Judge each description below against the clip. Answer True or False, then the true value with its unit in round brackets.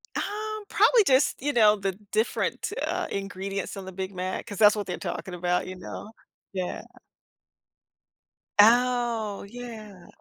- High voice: True (205 Hz)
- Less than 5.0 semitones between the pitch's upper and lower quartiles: True (4.3 semitones)